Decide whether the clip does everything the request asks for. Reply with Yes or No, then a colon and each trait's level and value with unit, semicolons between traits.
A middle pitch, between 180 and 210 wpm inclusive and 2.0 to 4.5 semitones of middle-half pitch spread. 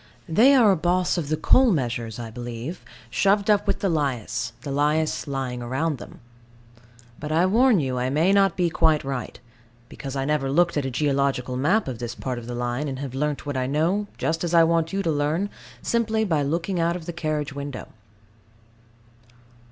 No: medium, 150 Hz; average, 200 wpm; average, 4.9 semitones